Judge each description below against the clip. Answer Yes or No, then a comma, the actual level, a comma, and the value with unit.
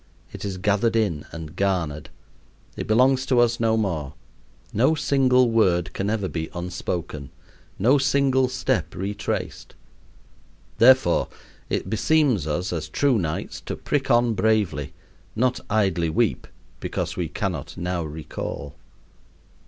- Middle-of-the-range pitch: No, low, 105 Hz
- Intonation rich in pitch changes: Yes, wide, 6.3 semitones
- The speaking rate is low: Yes, slow, 130 wpm